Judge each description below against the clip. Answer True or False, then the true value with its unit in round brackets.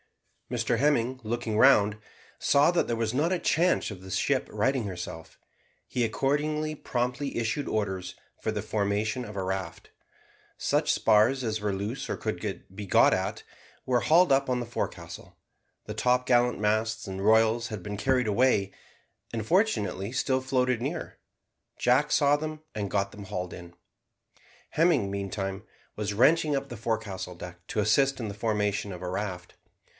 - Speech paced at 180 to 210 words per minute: False (160 wpm)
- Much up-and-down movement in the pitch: False (4.5 semitones)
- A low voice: True (110 Hz)